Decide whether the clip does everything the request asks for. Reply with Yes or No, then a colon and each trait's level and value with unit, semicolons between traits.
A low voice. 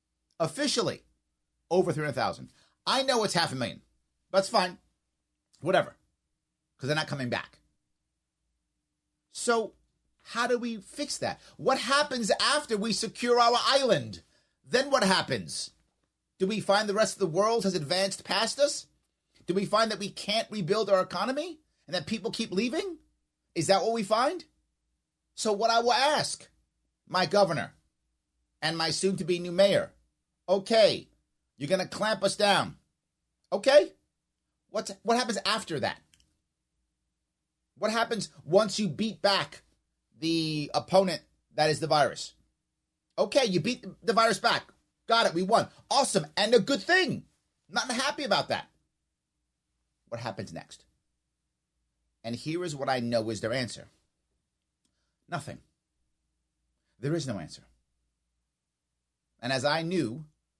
No: medium, 170 Hz